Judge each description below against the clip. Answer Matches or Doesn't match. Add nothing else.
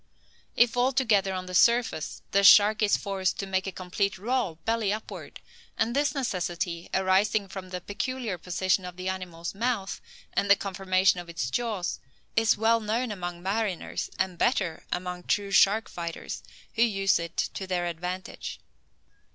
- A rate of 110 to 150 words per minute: Doesn't match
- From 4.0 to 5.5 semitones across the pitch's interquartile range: Doesn't match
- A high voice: Matches